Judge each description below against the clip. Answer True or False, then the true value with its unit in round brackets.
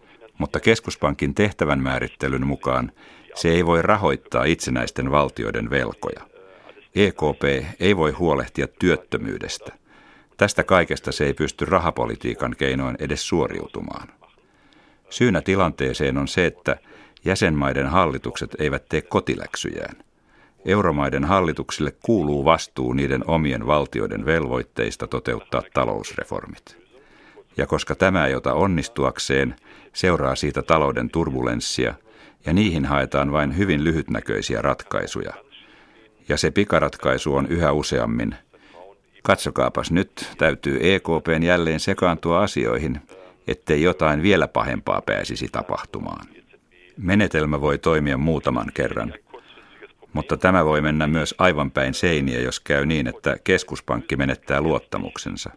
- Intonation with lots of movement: False (3.4 semitones)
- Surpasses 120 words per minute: False (110 wpm)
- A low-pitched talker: True (75 Hz)